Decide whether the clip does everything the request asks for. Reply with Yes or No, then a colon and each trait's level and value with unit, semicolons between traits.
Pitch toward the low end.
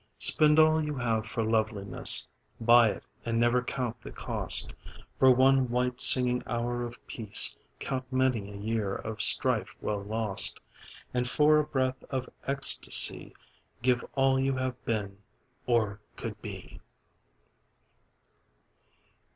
Yes: low, 120 Hz